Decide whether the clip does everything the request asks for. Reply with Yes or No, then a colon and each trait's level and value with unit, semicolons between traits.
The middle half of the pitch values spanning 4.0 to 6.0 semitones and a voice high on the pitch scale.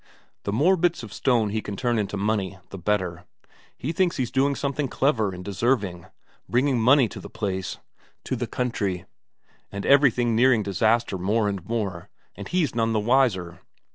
No: average, 4.8 semitones; low, 115 Hz